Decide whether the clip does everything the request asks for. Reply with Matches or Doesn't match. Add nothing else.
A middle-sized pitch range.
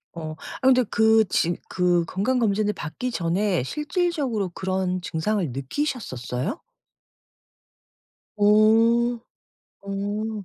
Matches